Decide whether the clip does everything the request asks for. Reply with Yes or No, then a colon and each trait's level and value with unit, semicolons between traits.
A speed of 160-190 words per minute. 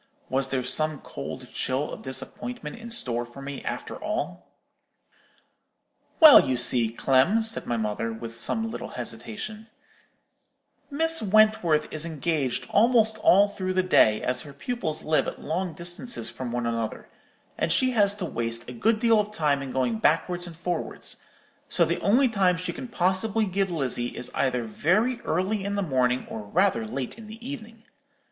Yes: average, 170 wpm